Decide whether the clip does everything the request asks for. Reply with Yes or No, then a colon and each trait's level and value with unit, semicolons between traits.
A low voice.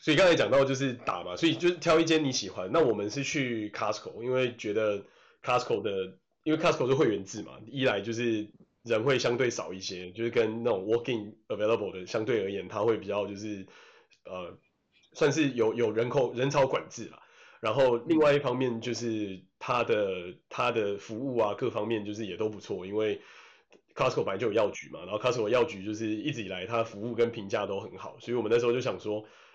Yes: low, 115 Hz